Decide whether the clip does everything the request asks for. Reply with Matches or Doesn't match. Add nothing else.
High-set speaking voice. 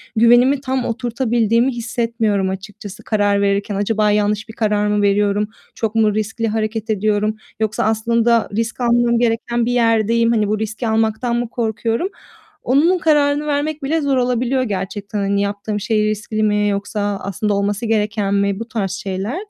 Matches